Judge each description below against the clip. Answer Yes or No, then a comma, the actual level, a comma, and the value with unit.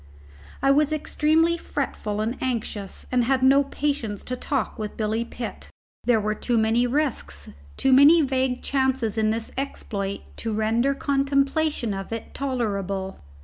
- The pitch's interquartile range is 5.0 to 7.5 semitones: No, average, 4.2 semitones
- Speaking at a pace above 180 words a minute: No, average, 145 wpm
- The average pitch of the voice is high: Yes, high, 245 Hz